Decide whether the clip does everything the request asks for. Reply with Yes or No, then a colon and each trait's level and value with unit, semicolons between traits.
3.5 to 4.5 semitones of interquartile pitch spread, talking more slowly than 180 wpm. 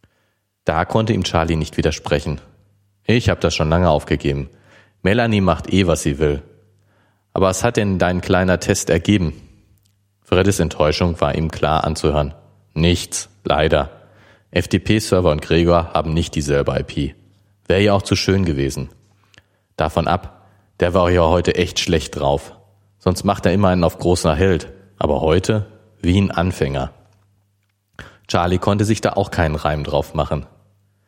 Yes: average, 3.9 semitones; average, 150 wpm